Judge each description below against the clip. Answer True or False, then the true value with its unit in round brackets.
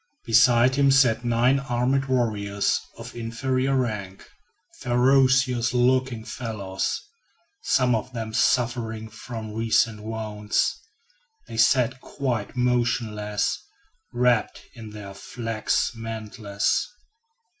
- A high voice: False (115 Hz)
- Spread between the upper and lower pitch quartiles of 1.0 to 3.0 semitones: True (2.5 semitones)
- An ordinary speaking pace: False (95 wpm)